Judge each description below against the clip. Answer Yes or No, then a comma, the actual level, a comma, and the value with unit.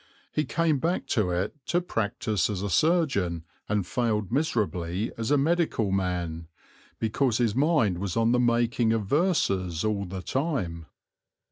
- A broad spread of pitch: Yes, wide, 6.9 semitones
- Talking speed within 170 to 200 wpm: No, average, 150 wpm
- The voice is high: No, low, 110 Hz